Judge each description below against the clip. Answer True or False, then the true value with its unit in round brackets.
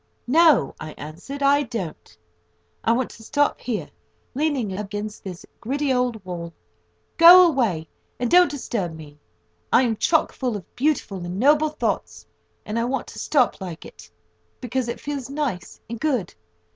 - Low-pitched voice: False (240 Hz)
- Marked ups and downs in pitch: True (6.9 semitones)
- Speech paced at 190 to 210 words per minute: False (160 wpm)